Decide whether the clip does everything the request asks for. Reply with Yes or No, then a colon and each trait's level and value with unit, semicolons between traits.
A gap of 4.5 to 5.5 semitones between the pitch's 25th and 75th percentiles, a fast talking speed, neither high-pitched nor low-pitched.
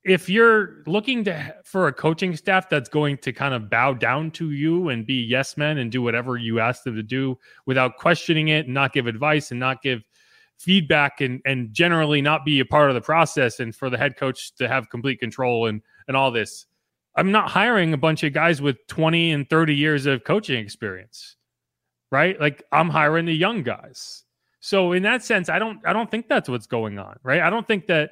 Yes: average, 5.2 semitones; fast, 220 wpm; medium, 150 Hz